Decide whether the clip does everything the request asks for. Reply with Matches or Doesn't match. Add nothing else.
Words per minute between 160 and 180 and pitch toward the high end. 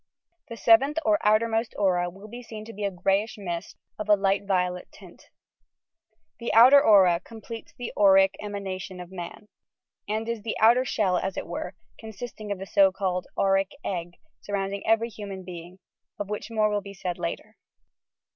Matches